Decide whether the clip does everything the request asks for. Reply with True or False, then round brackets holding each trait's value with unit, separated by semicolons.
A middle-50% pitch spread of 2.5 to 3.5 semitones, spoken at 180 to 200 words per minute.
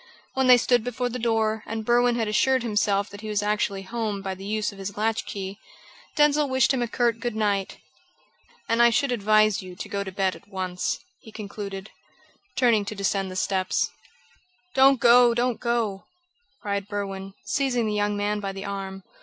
True (3.1 semitones; 190 wpm)